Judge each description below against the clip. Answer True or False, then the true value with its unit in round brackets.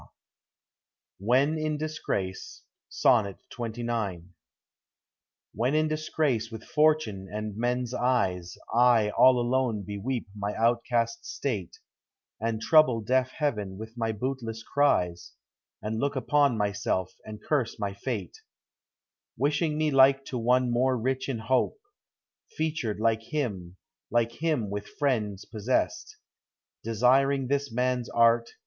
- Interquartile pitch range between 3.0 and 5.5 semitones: True (4.0 semitones)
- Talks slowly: True (125 wpm)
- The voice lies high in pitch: False (120 Hz)